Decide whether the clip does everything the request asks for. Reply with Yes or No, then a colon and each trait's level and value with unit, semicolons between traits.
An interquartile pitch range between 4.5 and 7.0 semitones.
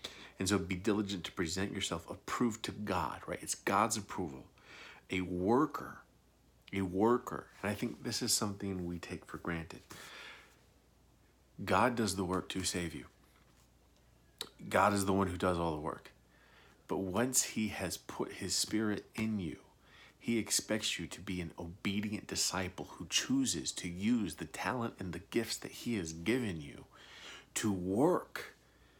No: average, 3.3 semitones